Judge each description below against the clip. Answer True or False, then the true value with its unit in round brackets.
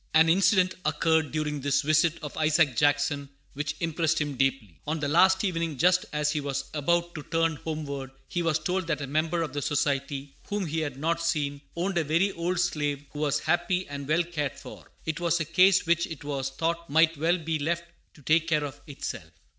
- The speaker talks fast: True (210 wpm)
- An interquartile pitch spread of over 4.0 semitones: False (2.7 semitones)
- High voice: False (155 Hz)